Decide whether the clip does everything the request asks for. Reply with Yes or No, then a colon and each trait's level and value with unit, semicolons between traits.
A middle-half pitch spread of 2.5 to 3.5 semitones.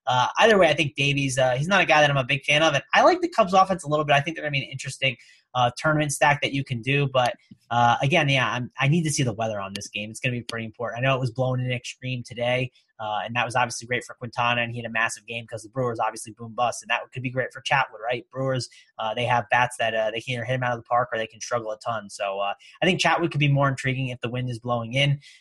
Yes: average, 2.9 semitones